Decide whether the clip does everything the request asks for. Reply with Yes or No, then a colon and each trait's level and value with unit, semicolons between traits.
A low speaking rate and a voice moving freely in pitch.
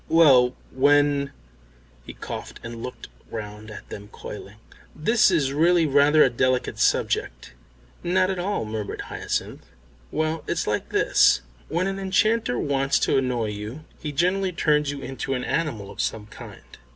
No: average, 155 wpm; wide, 6.6 semitones